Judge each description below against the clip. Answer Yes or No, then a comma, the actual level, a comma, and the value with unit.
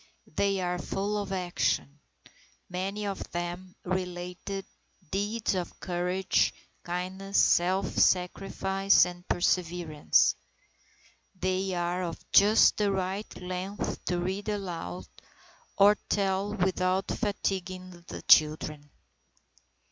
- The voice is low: No, medium, 185 Hz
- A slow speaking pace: Yes, slow, 100 wpm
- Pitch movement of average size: No, narrow, 1.8 semitones